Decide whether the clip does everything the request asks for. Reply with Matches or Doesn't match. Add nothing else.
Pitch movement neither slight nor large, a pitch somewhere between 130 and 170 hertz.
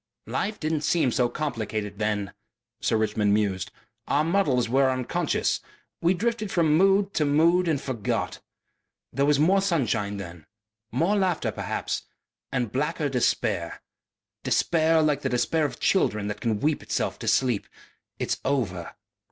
Doesn't match